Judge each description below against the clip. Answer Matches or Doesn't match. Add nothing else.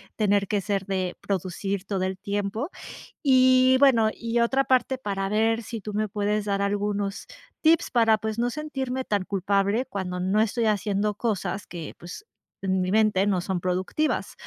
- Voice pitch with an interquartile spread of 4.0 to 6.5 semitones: Doesn't match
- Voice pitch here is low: Doesn't match